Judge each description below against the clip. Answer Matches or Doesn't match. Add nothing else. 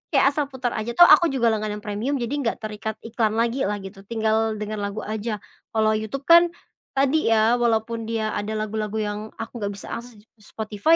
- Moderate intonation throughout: Doesn't match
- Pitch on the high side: Matches